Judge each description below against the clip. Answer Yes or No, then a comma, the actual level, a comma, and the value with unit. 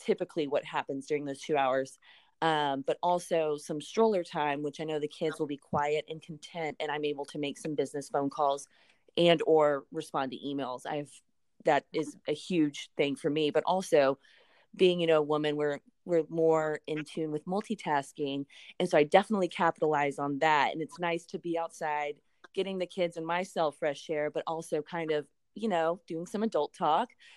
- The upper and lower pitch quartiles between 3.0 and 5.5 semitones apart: No, narrow, 2.5 semitones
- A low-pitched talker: No, medium, 155 Hz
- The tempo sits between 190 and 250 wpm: Yes, average, 195 wpm